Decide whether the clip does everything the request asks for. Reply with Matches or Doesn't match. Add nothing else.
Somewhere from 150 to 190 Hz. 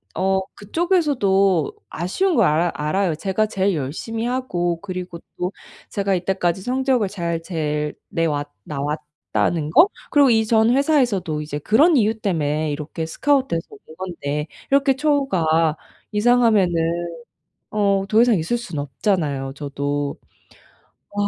Matches